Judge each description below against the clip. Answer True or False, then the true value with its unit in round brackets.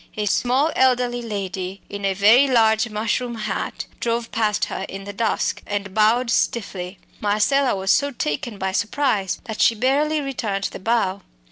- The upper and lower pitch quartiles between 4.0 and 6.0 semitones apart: False (3.6 semitones)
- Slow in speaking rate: False (160 wpm)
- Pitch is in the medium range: False (220 Hz)